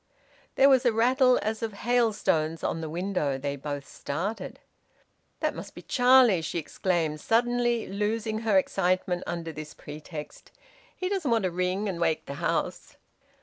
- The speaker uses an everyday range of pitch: No, wide, 6.2 semitones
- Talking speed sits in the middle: Yes, average, 155 wpm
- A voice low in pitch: No, high, 195 Hz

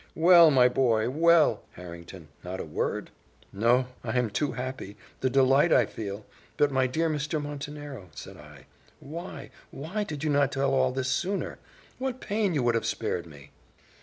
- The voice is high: No, low, 135 Hz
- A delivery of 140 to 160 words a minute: No, average, 170 wpm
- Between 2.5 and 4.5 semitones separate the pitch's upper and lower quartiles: No, wide, 5.6 semitones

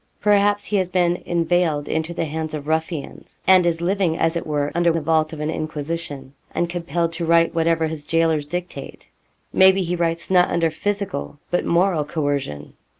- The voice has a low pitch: No, medium, 165 Hz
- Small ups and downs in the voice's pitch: Yes, narrow, 2.1 semitones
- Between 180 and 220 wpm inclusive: Yes, average, 185 wpm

